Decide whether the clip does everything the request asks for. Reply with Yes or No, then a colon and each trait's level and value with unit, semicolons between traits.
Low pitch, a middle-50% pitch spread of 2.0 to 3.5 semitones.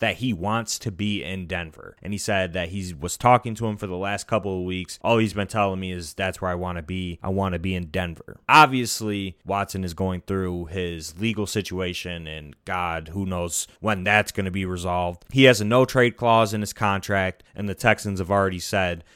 Yes: very low, 95 Hz; average, 2.8 semitones